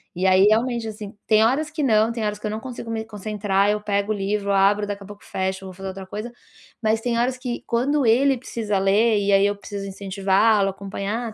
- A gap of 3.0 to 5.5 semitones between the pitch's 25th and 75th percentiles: No, narrow, 2.5 semitones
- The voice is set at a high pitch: Yes, high, 210 Hz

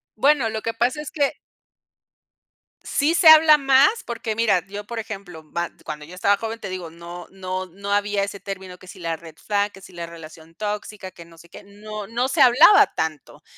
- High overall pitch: Yes, high, 200 Hz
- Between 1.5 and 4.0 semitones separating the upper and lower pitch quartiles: No, average, 4.8 semitones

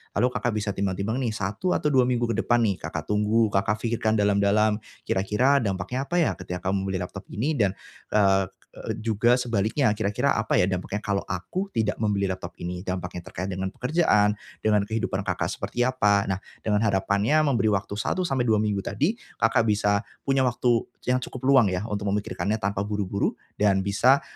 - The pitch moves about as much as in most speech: Yes, average, 3.4 semitones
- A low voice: Yes, low, 105 Hz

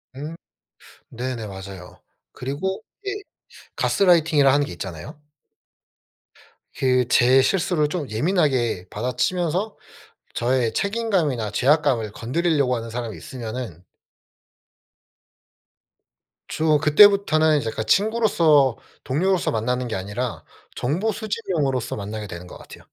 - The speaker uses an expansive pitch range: Yes, wide, 6.2 semitones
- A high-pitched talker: No, low, 135 Hz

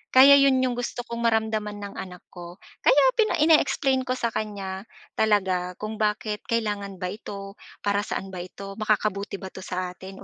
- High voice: Yes, high, 210 Hz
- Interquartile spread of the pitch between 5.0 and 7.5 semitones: No, average, 3.3 semitones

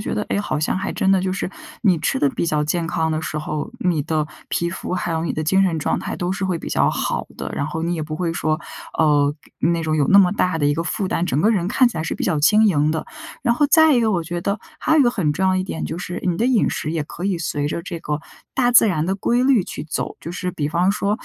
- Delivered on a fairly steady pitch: No, average, 3.9 semitones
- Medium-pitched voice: Yes, medium, 175 Hz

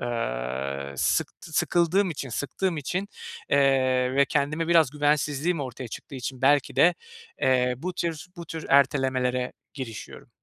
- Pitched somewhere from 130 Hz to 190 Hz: Yes, medium, 140 Hz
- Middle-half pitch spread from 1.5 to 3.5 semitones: No, average, 4.2 semitones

